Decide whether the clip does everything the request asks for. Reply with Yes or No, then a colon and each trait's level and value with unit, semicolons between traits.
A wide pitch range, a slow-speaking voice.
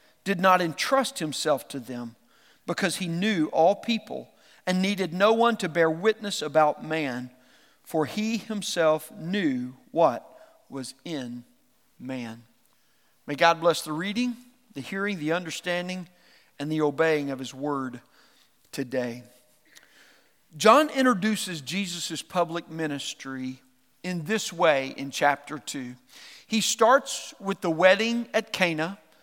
Yes: wide, 6.6 semitones; slow, 125 wpm